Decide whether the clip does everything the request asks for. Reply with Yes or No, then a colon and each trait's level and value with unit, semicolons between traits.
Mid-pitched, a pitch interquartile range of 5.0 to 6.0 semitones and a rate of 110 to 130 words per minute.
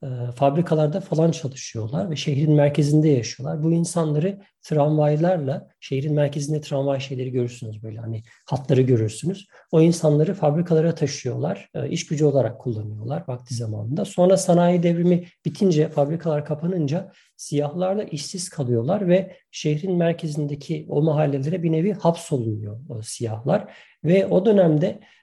No: medium, 150 Hz; average, 4.0 semitones; average, 120 wpm